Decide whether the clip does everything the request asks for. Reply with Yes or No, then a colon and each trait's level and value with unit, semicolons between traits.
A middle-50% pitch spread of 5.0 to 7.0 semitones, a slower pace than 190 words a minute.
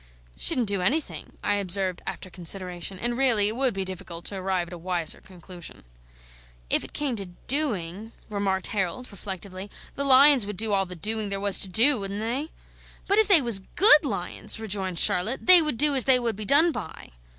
No: wide, 5.5 semitones; average, 195 wpm